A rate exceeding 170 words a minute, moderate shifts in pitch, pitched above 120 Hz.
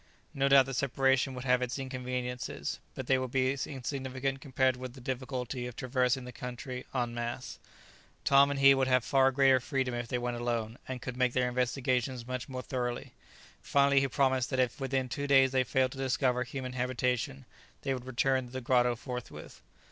No: average, 195 wpm; narrow, 1.3 semitones; low, 130 Hz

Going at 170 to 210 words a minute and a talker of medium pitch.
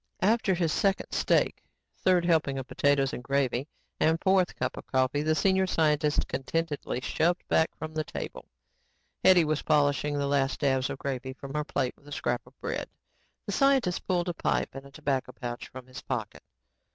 Yes: average, 180 wpm; medium, 145 Hz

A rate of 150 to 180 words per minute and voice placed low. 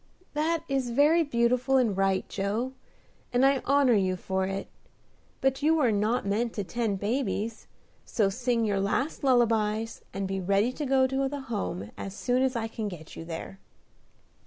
No: average, 175 wpm; high, 230 Hz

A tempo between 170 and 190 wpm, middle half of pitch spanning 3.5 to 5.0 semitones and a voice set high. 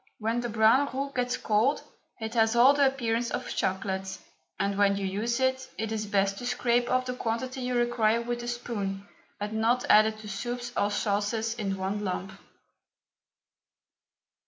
No: average, 175 wpm; average, 3.0 semitones; high, 225 Hz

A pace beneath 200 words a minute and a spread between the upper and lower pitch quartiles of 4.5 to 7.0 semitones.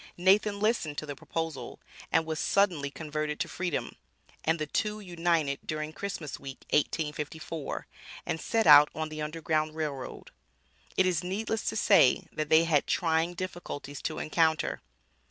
No: average, 155 wpm; average, 2.8 semitones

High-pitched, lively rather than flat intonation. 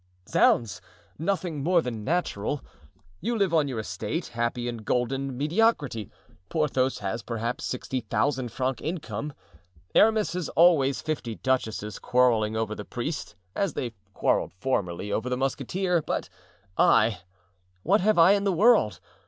No: low, 130 Hz; wide, 6.8 semitones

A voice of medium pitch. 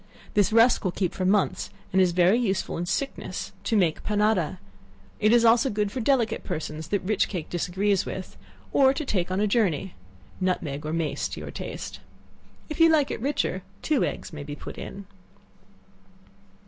No: high, 200 Hz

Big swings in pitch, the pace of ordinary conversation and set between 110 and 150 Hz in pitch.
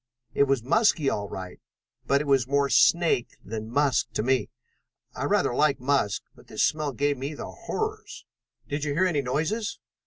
No: average, 3.3 semitones; average, 180 wpm; medium, 140 Hz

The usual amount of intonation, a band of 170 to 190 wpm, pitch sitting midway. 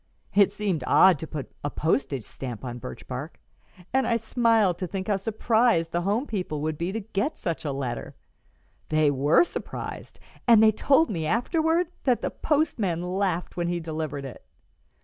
No: wide, 6.3 semitones; average, 175 wpm; medium, 180 Hz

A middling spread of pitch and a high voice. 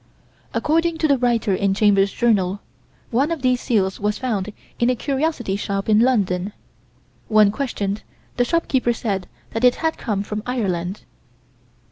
Yes: average, 4.3 semitones; high, 220 Hz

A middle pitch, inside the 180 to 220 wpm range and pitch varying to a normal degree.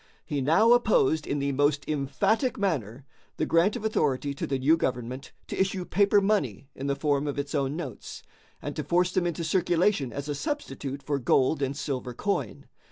Yes: medium, 145 Hz; average, 190 wpm; average, 4.8 semitones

